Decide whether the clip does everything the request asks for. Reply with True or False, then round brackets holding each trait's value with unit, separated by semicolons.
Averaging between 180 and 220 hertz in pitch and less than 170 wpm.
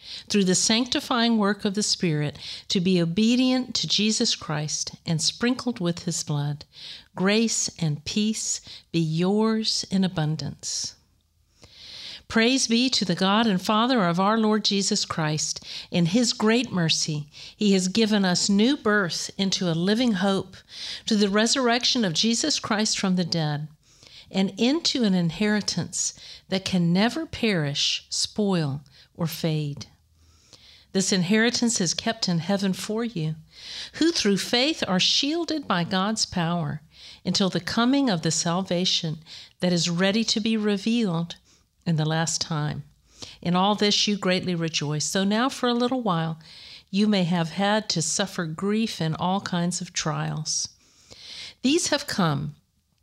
True (190 Hz; 145 wpm)